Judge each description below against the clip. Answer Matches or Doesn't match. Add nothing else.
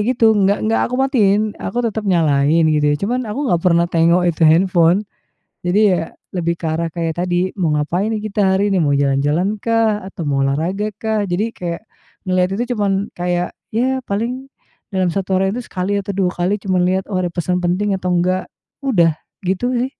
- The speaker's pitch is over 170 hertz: Matches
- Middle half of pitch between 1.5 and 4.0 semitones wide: Matches